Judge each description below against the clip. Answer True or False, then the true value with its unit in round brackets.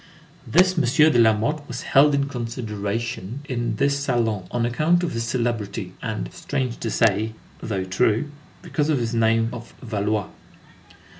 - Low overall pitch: True (115 Hz)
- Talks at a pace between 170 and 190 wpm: False (150 wpm)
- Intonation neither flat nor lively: True (4.2 semitones)